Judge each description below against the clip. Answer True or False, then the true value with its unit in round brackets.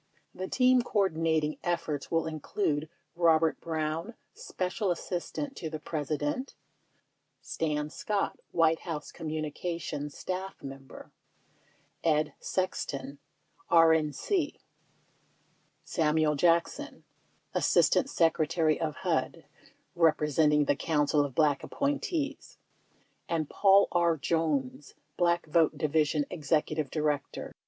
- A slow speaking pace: True (100 wpm)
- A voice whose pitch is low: False (160 Hz)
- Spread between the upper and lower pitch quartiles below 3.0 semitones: True (2.5 semitones)